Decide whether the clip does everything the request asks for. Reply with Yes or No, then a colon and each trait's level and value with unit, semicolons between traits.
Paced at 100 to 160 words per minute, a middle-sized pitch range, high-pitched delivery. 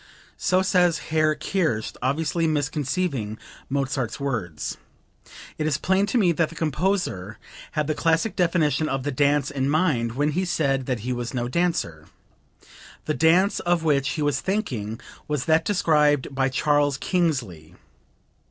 No: average, 150 wpm; average, 4.0 semitones; medium, 150 Hz